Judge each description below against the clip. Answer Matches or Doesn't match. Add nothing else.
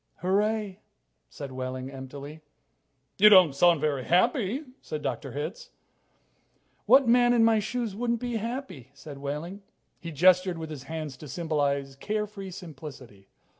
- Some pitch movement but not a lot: Doesn't match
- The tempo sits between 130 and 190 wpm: Matches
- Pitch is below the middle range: Doesn't match